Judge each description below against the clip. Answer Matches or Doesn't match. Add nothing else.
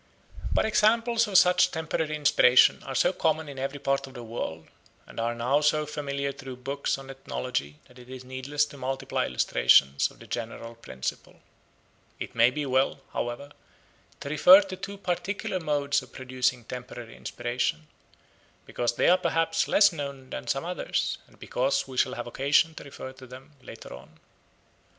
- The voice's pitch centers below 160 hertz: Matches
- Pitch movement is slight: Doesn't match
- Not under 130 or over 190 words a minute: Matches